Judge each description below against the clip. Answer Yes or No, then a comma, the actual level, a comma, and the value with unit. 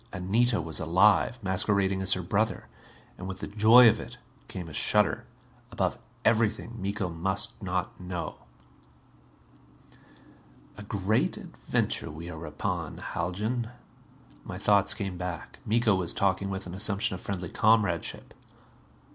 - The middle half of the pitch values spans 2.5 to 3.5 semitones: Yes, average, 2.9 semitones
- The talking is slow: Yes, slow, 130 wpm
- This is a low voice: Yes, very low, 95 Hz